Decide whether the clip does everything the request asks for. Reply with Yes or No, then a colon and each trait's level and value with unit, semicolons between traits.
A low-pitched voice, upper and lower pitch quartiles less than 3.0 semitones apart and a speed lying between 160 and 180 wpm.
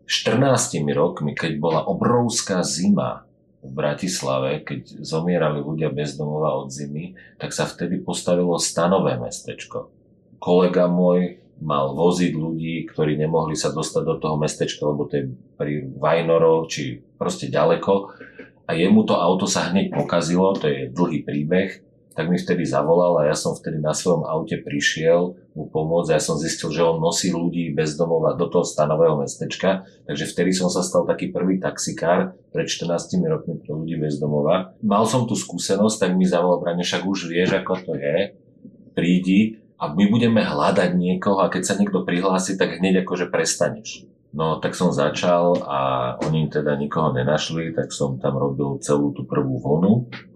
No: very low, 85 Hz; average, 3.6 semitones; fast, 165 wpm